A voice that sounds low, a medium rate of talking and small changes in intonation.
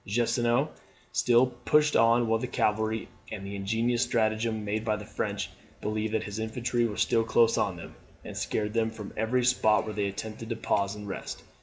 Yes: low, 110 Hz; average, 190 wpm; narrow, 1.9 semitones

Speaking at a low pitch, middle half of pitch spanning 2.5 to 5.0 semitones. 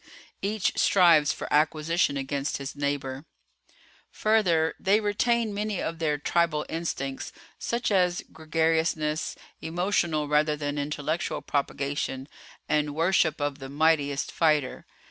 No: medium, 155 Hz; average, 3.2 semitones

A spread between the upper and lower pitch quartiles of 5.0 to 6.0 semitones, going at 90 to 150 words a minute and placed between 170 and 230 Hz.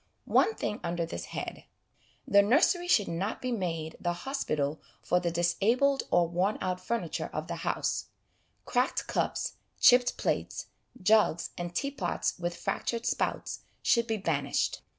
Yes: wide, 5.6 semitones; average, 145 wpm; medium, 185 Hz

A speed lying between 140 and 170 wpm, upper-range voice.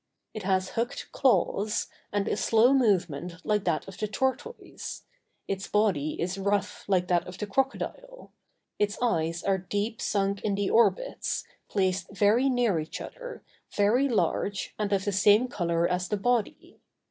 Yes: average, 160 wpm; high, 205 Hz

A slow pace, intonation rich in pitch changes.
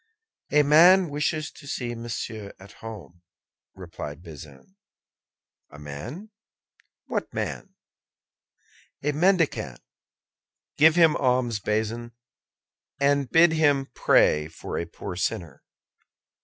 Yes: slow, 100 wpm; wide, 7.5 semitones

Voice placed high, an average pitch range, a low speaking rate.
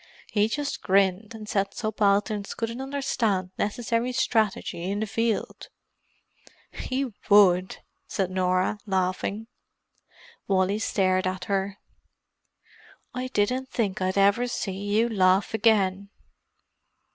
Yes: high, 205 Hz; average, 3.1 semitones; slow, 110 wpm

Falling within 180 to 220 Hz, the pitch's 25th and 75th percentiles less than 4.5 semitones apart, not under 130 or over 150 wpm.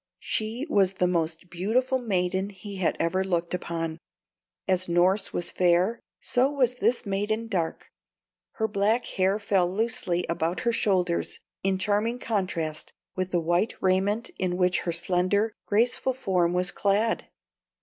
Yes: high, 190 Hz; average, 3.5 semitones; average, 145 wpm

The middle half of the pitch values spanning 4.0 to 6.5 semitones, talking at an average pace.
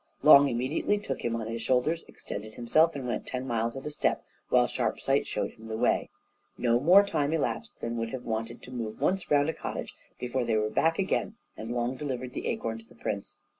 No: average, 4.4 semitones; fast, 220 wpm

